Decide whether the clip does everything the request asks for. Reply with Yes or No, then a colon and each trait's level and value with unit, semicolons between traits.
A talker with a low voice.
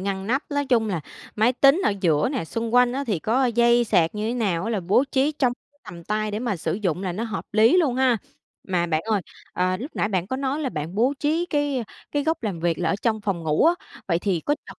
No: high, 220 Hz